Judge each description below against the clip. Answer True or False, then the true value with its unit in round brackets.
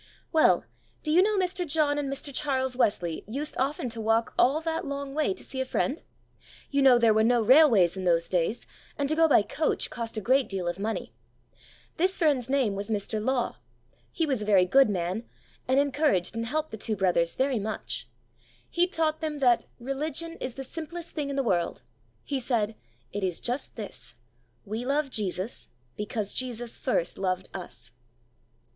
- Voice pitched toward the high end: True (250 Hz)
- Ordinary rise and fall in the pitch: False (5.7 semitones)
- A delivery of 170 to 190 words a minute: True (185 wpm)